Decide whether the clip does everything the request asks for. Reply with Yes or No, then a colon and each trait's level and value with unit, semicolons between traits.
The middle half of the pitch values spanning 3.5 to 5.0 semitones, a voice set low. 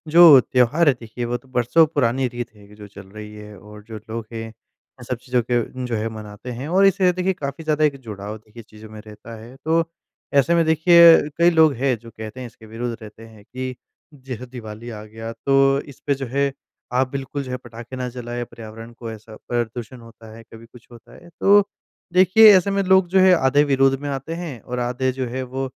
Yes: average, 4.0 semitones; low, 125 Hz